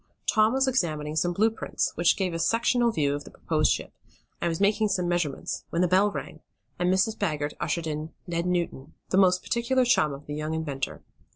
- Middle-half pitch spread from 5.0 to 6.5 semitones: Yes, average, 5.3 semitones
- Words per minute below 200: No, fast, 205 wpm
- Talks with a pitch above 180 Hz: No, medium, 175 Hz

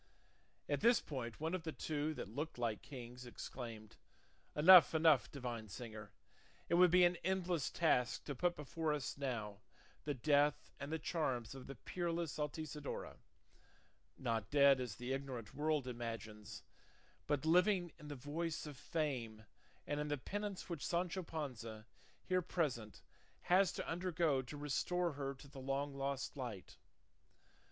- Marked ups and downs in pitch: No, average, 4.9 semitones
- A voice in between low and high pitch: Yes, medium, 145 Hz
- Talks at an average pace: Yes, average, 150 wpm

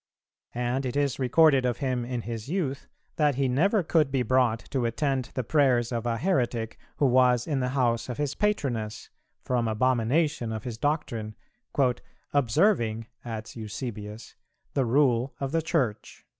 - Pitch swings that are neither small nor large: Yes, average, 3.4 semitones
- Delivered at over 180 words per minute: No, average, 155 wpm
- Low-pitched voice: Yes, low, 125 Hz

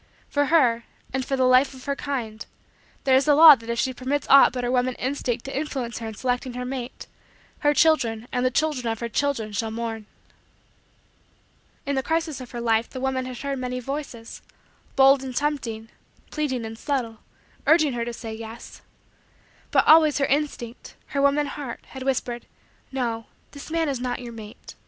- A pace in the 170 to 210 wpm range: Yes, average, 190 wpm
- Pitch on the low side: No, very high, 255 Hz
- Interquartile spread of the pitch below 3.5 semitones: Yes, average, 3.1 semitones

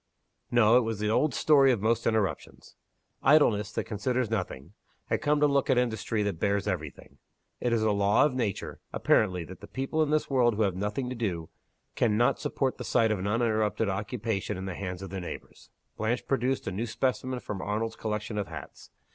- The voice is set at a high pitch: No, low, 110 Hz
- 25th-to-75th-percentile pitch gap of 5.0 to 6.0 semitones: No, average, 3.7 semitones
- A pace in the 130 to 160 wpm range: No, fast, 205 wpm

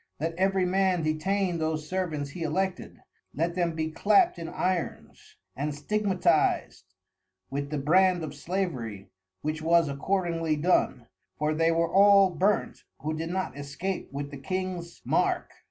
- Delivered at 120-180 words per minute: Yes, average, 145 wpm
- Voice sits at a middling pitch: Yes, medium, 165 Hz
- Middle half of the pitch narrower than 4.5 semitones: Yes, average, 3.5 semitones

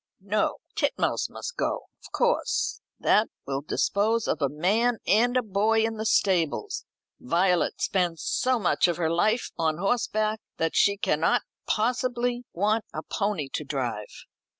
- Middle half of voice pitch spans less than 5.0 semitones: No, wide, 5.4 semitones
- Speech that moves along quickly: No, average, 150 wpm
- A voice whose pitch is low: No, high, 205 Hz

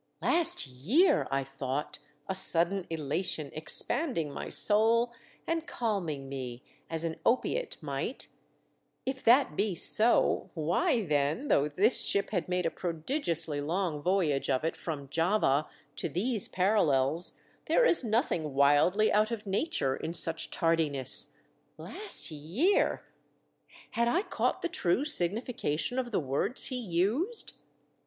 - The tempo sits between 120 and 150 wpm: Yes, slow, 135 wpm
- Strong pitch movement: Yes, wide, 7.6 semitones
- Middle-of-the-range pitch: Yes, medium, 180 Hz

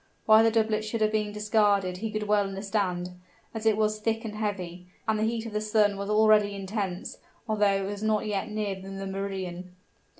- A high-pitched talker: Yes, high, 210 Hz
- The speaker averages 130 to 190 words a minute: No, average, 200 wpm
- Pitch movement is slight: Yes, narrow, 1.8 semitones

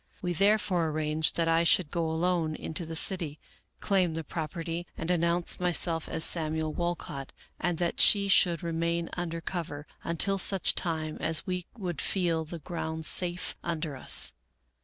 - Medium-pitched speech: Yes, medium, 170 Hz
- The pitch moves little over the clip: Yes, narrow, 1.8 semitones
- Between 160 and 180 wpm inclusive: Yes, average, 165 wpm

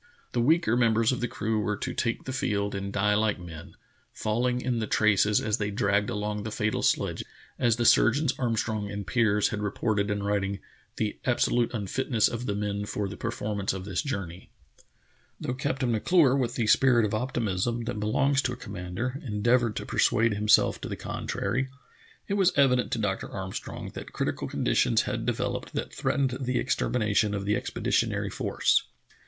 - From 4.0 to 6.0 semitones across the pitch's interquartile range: No, average, 3.3 semitones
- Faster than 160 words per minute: Yes, average, 180 wpm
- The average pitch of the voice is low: Yes, low, 110 Hz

